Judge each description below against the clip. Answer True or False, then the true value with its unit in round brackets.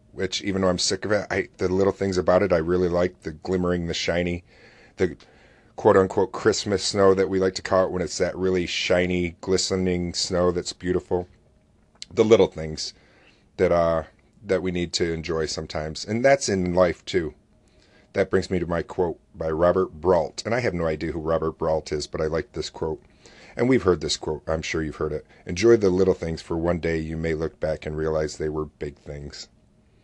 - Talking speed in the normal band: False (210 wpm)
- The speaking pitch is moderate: False (90 Hz)